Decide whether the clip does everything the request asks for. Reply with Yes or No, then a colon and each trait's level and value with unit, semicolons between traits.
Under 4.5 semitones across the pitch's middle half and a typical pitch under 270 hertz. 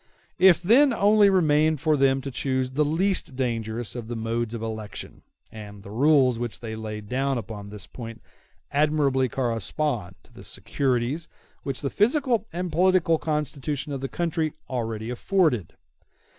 No: wide, 5.5 semitones; low, 135 Hz